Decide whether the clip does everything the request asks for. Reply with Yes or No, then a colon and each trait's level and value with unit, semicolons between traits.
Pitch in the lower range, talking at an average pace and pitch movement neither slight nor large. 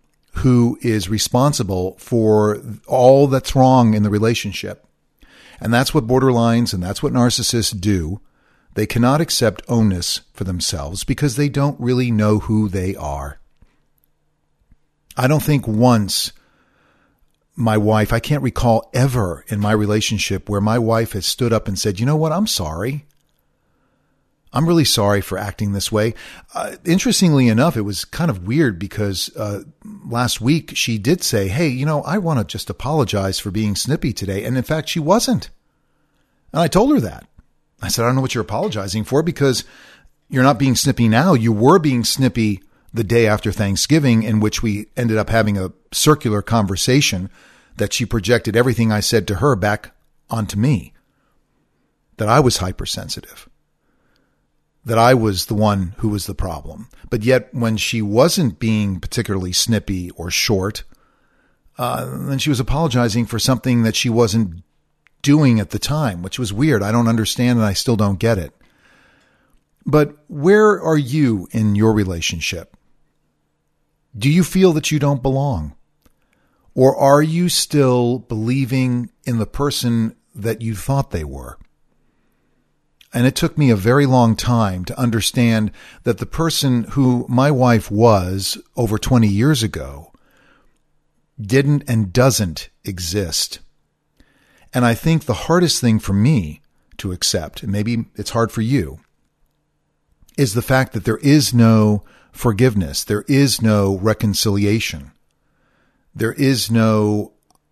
Yes: low, 115 Hz; average, 155 wpm; average, 4.2 semitones